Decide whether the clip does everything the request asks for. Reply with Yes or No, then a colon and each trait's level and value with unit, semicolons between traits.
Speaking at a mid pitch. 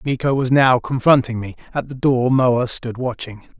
No: low, 125 Hz